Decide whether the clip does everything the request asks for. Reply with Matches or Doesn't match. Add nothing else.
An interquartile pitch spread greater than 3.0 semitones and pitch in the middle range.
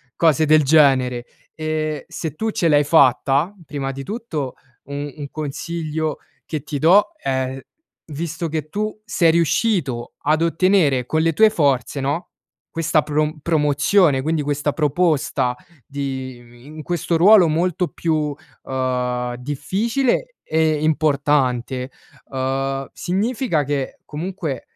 Matches